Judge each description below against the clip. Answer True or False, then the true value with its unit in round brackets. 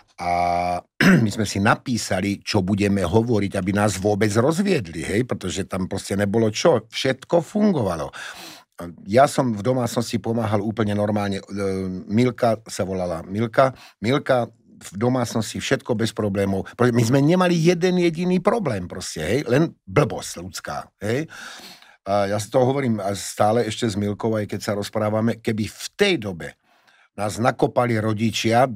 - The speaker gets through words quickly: False (140 wpm)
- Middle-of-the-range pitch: False (110 Hz)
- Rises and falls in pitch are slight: False (3.9 semitones)